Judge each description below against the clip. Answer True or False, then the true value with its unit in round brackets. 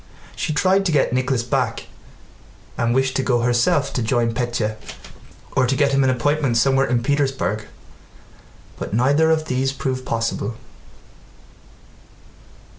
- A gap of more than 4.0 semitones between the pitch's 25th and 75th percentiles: False (2.7 semitones)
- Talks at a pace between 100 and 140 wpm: True (135 wpm)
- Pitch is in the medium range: False (130 Hz)